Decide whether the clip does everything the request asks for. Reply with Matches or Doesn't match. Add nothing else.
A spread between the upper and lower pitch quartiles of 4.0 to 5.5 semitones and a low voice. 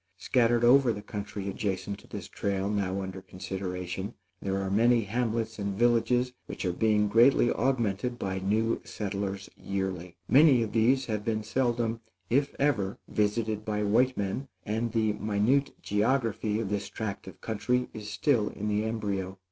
Doesn't match